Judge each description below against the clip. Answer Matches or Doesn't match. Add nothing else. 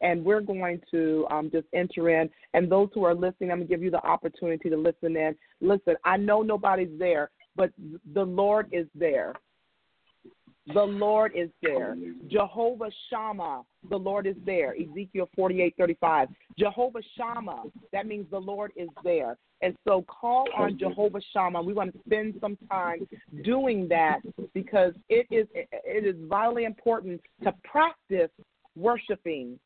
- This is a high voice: Matches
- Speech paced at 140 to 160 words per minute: Matches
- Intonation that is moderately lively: Matches